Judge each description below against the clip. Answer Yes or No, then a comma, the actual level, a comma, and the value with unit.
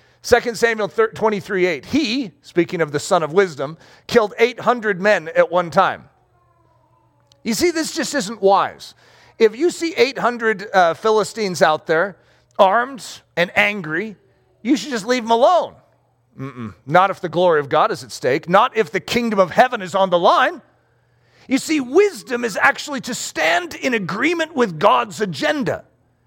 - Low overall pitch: No, high, 210 Hz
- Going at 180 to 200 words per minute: No, average, 165 wpm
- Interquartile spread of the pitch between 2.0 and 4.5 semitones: No, average, 5.3 semitones